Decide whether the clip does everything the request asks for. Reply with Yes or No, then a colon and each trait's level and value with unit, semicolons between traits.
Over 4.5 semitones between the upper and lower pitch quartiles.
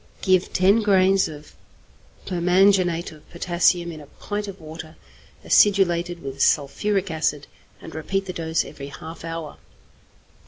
No: average, 3.3 semitones